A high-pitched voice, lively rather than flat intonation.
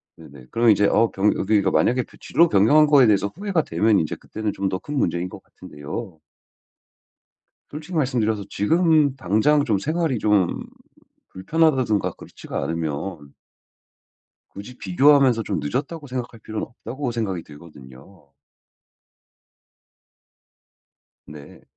No: low, 110 Hz; wide, 6.9 semitones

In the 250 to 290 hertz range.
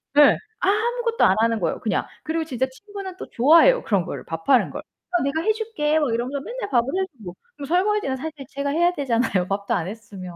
Yes: very high, 285 Hz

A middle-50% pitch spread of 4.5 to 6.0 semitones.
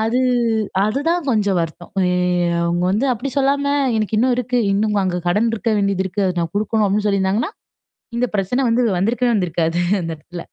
Yes: average, 5.0 semitones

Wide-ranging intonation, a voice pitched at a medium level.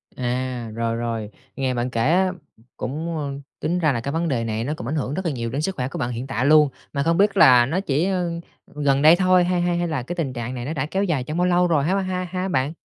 Yes: wide, 5.7 semitones; medium, 150 Hz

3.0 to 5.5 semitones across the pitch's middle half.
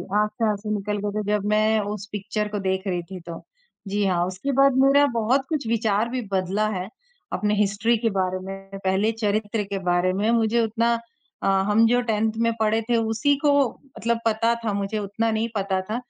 No: narrow, 2.5 semitones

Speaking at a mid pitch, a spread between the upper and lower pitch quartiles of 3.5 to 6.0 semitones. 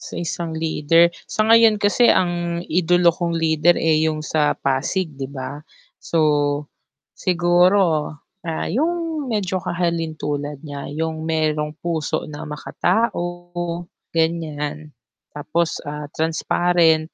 No: medium, 165 Hz; narrow, 2.4 semitones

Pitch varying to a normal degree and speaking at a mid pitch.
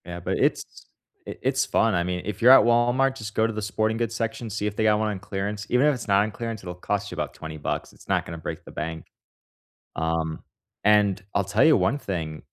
No: average, 4.2 semitones; low, 105 Hz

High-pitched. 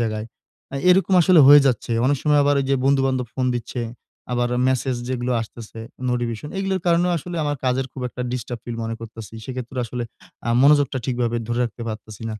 No: low, 125 Hz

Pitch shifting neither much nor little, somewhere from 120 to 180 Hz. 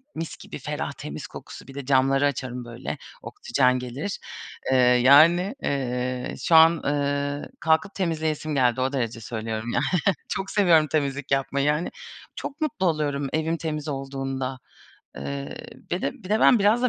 Yes: average, 3.9 semitones; medium, 140 Hz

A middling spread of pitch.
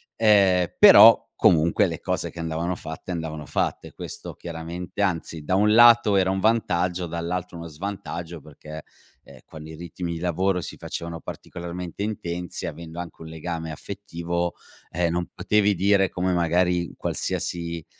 No: narrow, 2.0 semitones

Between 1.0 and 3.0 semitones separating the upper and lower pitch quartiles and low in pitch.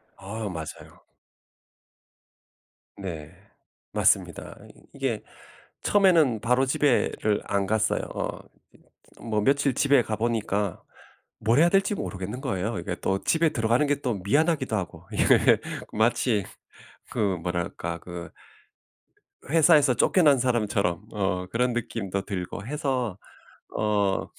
No: wide, 5.5 semitones; low, 110 Hz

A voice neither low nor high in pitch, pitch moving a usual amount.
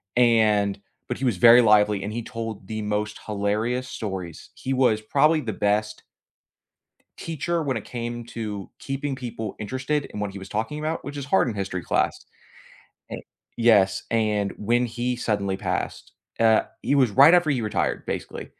No: low, 115 Hz; average, 3.6 semitones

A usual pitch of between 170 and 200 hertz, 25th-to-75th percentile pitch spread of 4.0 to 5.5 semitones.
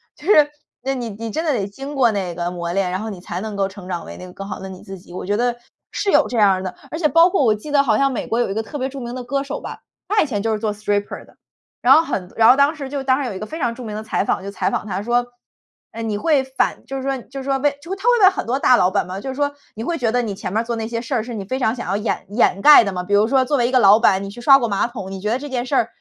No: high, 230 Hz; average, 5.2 semitones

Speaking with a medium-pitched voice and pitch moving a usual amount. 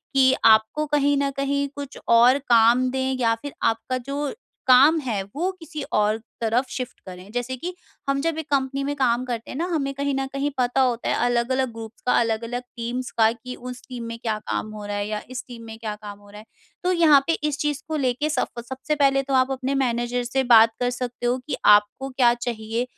No: very high, 250 Hz; average, 3.1 semitones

